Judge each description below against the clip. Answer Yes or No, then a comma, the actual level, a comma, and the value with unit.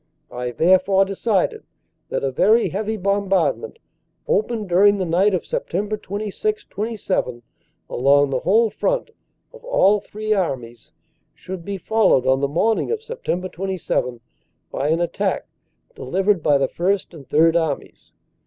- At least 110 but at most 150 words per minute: Yes, average, 140 wpm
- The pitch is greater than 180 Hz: Yes, high, 190 Hz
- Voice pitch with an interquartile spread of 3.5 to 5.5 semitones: Yes, average, 5.1 semitones